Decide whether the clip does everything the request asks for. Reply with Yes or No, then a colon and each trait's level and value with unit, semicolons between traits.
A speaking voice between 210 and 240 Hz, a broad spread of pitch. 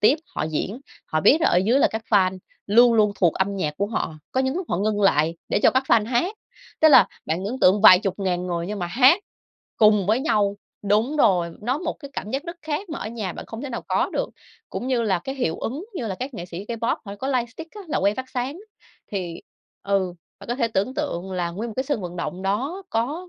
Yes: high, 215 Hz; wide, 5.7 semitones